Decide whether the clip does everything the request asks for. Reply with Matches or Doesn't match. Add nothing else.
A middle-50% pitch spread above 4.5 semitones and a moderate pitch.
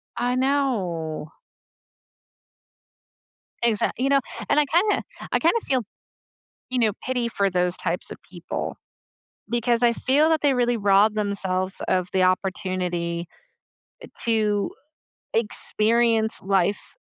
Doesn't match